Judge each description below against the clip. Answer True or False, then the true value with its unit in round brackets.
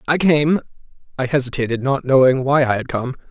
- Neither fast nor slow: True (165 wpm)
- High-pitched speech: False (135 Hz)